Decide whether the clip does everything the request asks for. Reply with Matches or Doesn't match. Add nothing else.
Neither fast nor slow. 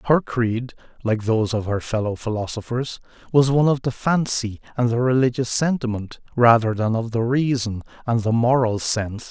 Matches